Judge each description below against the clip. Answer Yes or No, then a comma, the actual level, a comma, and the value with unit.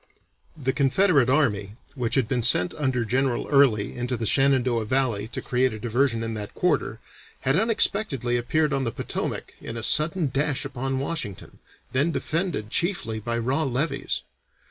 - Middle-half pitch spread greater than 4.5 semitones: No, average, 3.6 semitones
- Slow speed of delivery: No, average, 160 wpm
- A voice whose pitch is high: No, low, 130 Hz